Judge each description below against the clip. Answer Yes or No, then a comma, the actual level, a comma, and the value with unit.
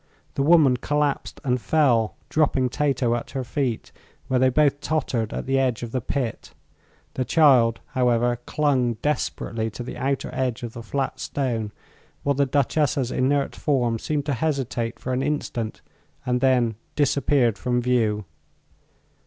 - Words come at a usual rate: Yes, average, 155 wpm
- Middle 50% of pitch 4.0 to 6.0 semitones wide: No, average, 3.0 semitones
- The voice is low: Yes, low, 130 Hz